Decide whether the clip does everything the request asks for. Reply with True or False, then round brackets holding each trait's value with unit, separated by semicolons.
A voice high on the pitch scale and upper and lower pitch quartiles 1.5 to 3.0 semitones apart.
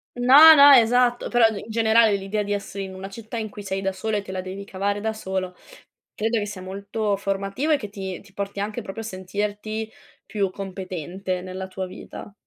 True (200 Hz; 2.4 semitones)